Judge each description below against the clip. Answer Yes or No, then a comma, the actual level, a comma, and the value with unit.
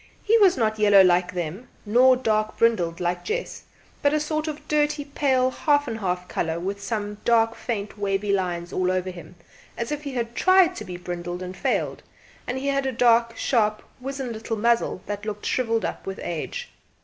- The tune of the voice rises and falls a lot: Yes, wide, 5.9 semitones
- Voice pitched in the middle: No, high, 225 Hz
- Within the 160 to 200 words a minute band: Yes, average, 195 wpm